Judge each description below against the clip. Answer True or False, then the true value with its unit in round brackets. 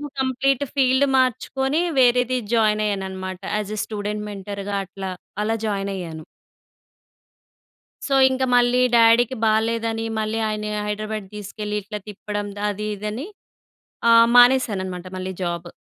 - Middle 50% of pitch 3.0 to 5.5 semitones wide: True (3.4 semitones)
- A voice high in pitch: True (215 Hz)